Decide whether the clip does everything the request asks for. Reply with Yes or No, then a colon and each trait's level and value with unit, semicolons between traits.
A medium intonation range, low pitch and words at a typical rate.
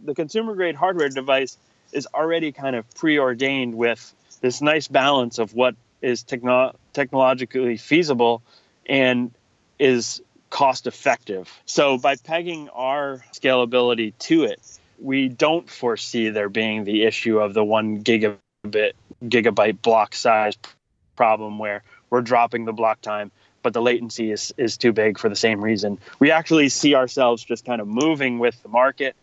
Yes: average, 3.5 semitones; low, 120 Hz; average, 150 wpm